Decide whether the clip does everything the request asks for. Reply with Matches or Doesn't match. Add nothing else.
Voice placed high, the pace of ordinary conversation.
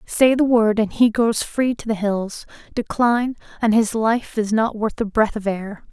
Doesn't match